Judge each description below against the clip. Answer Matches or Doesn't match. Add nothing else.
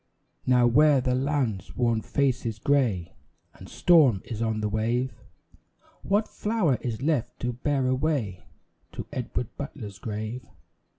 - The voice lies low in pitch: Matches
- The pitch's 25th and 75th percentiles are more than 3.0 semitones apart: Matches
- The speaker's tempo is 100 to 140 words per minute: Matches